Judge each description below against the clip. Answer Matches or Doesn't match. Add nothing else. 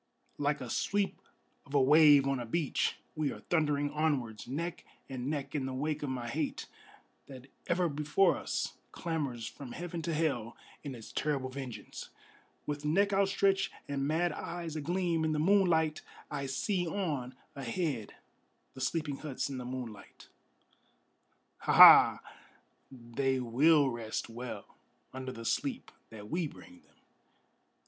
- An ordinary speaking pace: Matches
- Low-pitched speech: Doesn't match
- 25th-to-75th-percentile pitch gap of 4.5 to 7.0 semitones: Doesn't match